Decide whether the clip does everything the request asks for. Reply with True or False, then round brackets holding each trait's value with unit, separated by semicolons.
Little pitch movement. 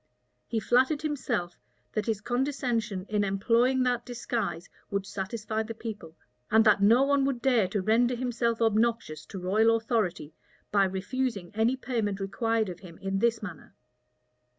False (3.6 semitones)